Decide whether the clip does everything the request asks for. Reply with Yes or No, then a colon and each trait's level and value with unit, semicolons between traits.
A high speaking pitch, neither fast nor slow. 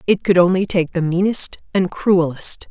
No: medium, 180 Hz; average, 180 wpm